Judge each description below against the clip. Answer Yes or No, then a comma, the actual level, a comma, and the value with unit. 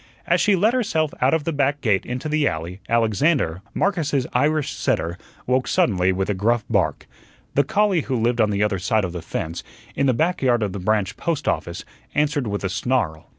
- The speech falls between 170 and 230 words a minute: Yes, fast, 205 wpm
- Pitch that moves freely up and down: Yes, wide, 7.4 semitones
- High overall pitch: No, low, 120 Hz